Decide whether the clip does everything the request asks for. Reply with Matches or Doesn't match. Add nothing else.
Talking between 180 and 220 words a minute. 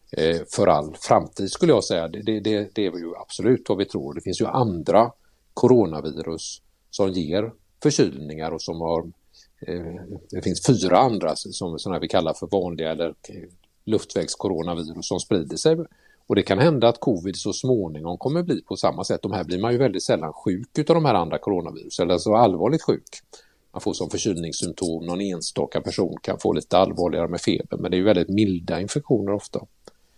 Matches